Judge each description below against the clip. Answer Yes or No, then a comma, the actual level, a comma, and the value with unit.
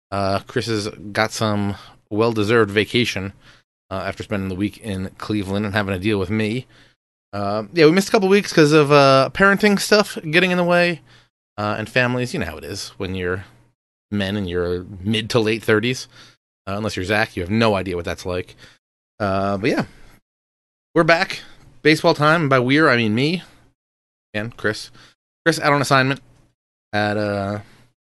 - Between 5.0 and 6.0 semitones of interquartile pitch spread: Yes, wide, 5.4 semitones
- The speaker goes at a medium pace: Yes, average, 180 wpm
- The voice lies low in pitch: Yes, low, 110 Hz